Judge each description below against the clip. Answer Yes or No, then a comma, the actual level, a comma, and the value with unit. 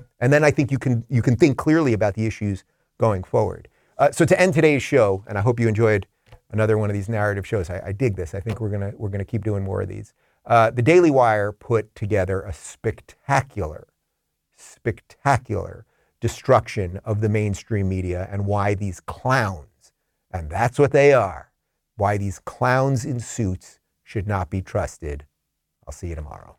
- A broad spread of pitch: No, average, 3.7 semitones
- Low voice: Yes, low, 105 Hz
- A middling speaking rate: Yes, average, 190 wpm